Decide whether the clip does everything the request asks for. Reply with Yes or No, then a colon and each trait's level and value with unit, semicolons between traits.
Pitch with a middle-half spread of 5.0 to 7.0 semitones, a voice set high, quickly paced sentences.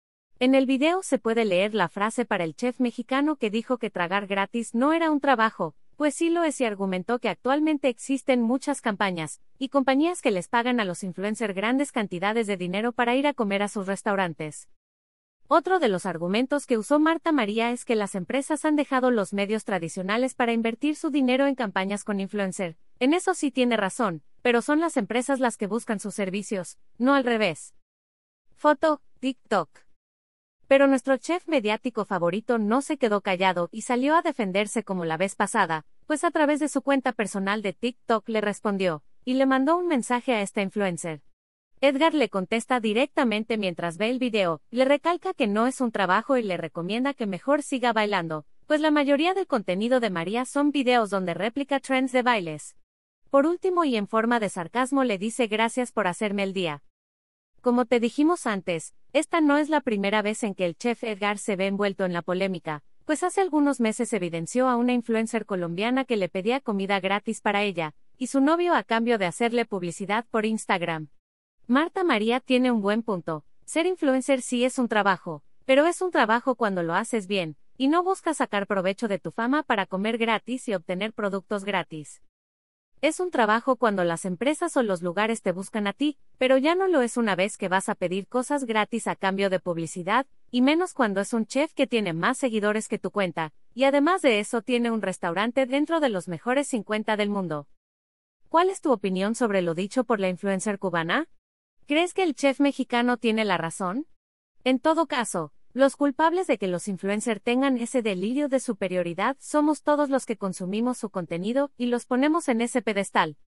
Yes: wide, 5.5 semitones; high, 230 Hz; fast, 195 wpm